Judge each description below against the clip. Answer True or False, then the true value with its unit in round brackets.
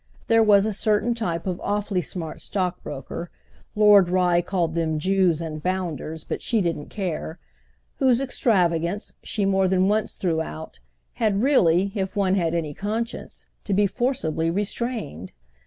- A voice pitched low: False (185 Hz)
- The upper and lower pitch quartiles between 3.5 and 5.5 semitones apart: True (3.9 semitones)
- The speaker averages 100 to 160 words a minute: True (140 wpm)